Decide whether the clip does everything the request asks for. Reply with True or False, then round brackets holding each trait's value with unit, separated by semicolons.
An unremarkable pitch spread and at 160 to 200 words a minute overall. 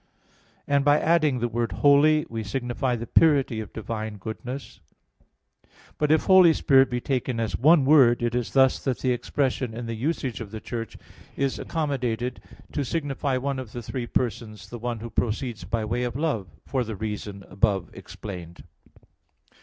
True (3.7 semitones; 170 wpm)